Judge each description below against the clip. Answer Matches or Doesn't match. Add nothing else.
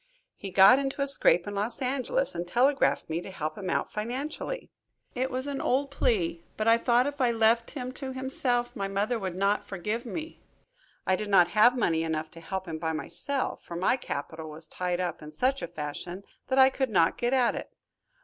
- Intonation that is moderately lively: Doesn't match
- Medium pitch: Doesn't match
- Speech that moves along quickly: Matches